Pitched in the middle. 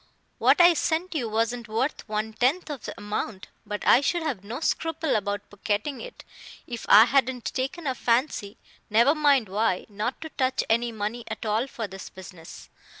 No: high, 235 Hz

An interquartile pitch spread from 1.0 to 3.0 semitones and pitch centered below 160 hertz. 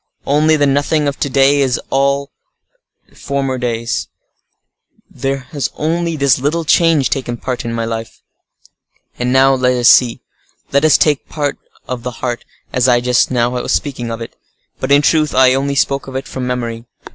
Yes: narrow, 2.4 semitones; low, 135 Hz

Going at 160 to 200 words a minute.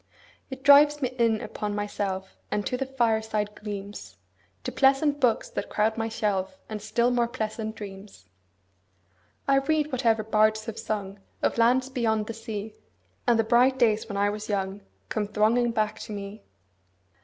Yes: average, 170 wpm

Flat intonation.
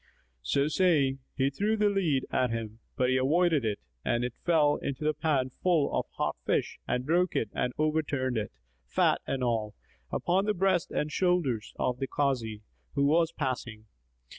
No: average, 4.9 semitones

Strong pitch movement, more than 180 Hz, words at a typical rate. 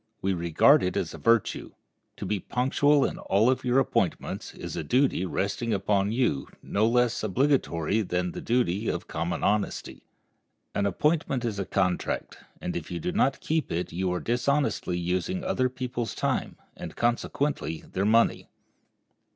No: wide, 5.8 semitones; low, 110 Hz; average, 160 wpm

